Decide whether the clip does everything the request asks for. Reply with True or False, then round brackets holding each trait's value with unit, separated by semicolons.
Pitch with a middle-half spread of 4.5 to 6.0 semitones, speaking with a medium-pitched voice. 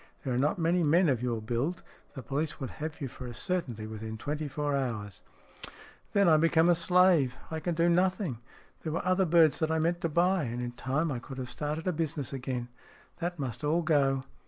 True (5.0 semitones; 150 Hz)